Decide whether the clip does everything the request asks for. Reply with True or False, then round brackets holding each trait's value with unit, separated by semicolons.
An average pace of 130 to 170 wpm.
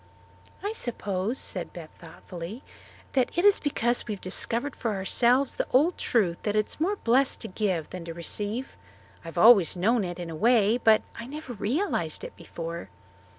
False (180 wpm)